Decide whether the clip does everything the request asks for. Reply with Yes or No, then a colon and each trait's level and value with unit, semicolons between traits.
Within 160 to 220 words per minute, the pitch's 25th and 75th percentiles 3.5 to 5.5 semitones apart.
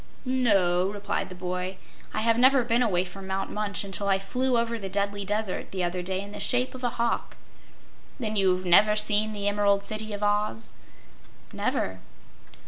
No: average, 180 wpm; narrow, 2.5 semitones